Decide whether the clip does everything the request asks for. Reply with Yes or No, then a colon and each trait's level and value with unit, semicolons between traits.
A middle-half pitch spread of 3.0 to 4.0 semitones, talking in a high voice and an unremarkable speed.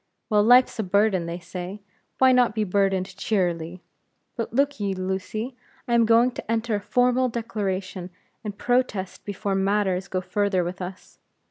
Yes: average, 3.7 semitones; high, 205 Hz; average, 160 wpm